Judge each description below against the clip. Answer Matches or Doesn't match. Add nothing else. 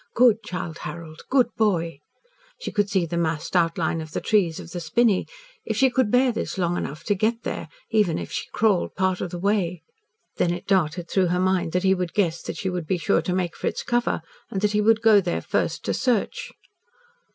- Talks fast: Matches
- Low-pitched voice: Doesn't match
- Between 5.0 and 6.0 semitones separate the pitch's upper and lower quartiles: Doesn't match